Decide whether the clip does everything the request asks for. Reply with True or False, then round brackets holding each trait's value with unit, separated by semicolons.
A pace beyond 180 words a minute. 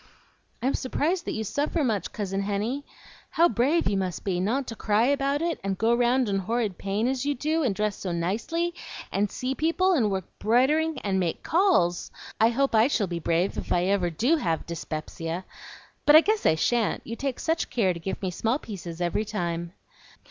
True (200 wpm)